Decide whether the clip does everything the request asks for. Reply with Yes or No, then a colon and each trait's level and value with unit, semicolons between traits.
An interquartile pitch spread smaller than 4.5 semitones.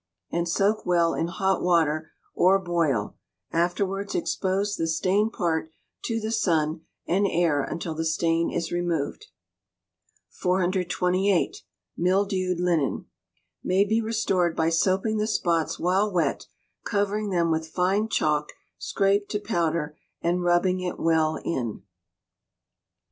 Yes: average, 3.0 semitones